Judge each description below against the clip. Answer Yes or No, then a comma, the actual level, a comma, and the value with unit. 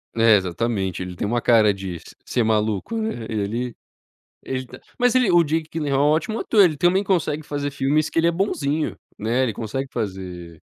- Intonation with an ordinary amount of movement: No, wide, 7.3 semitones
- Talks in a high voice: No, low, 130 Hz